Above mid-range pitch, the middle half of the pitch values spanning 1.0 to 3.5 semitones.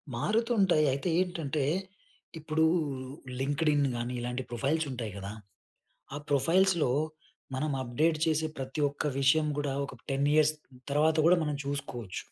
No: medium, 150 Hz; average, 3.0 semitones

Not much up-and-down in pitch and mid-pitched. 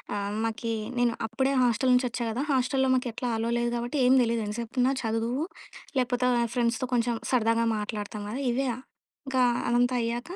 No: narrow, 1.8 semitones; high, 240 Hz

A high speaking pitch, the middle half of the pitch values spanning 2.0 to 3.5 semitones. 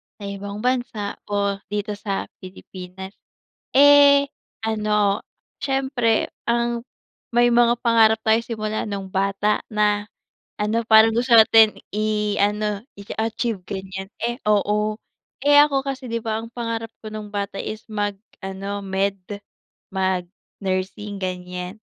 Yes: high, 210 Hz; narrow, 2.4 semitones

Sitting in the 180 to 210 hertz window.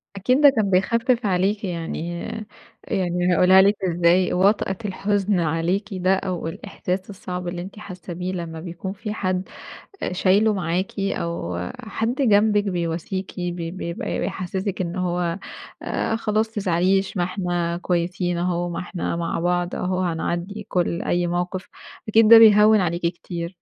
Yes: medium, 185 Hz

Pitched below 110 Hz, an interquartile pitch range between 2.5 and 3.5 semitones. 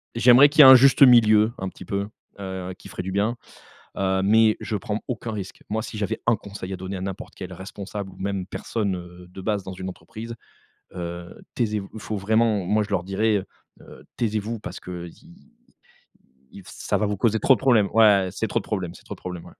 Yes: low, 100 Hz; average, 2.8 semitones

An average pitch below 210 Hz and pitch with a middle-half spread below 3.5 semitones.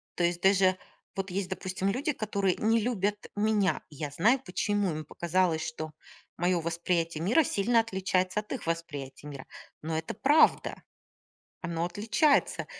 No: medium, 185 Hz; average, 3.8 semitones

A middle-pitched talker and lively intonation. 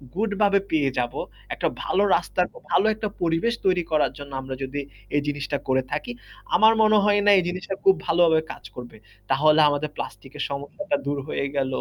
Yes: medium, 160 Hz; wide, 5.8 semitones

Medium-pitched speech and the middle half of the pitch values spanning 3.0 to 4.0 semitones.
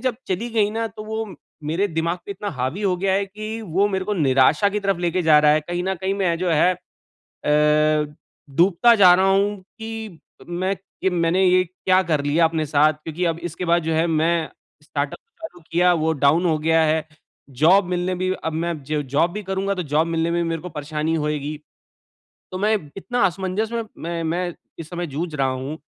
Yes: medium, 175 Hz; average, 3.5 semitones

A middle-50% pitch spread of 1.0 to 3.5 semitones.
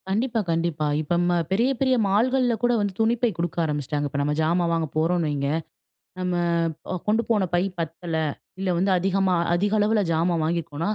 No: average, 4.4 semitones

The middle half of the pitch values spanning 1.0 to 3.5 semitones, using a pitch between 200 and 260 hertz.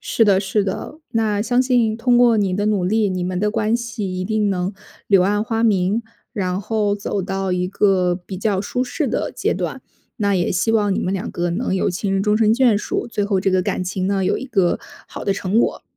Yes: average, 2.9 semitones; high, 205 Hz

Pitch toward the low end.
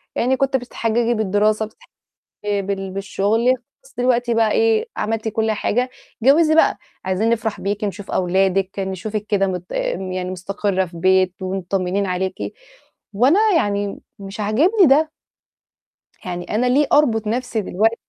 No: high, 210 Hz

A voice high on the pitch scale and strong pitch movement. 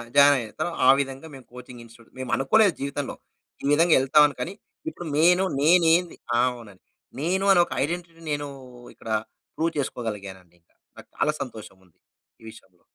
No: medium, 140 Hz; wide, 5.8 semitones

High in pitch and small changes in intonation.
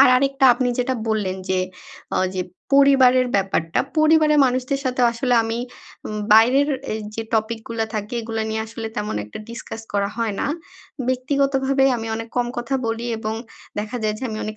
No: high, 230 Hz; average, 3.2 semitones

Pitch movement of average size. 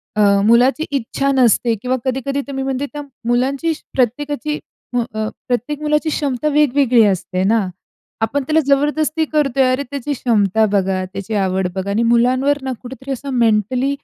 Yes: average, 4.1 semitones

